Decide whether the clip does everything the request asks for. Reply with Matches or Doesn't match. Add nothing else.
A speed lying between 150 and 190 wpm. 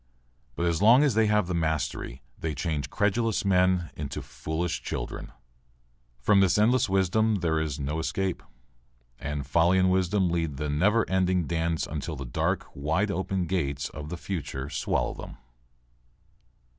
Matches